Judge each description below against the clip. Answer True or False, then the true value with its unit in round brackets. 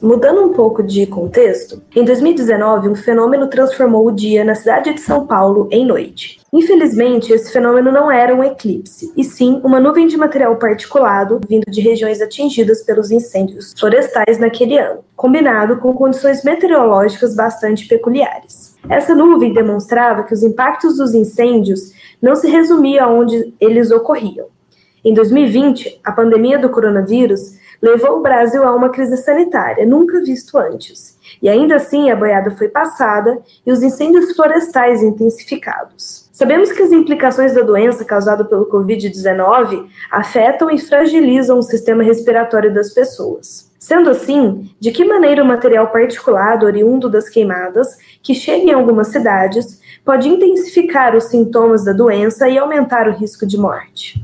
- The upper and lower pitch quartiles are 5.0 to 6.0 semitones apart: False (4.2 semitones)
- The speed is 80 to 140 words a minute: False (150 wpm)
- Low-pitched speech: False (240 Hz)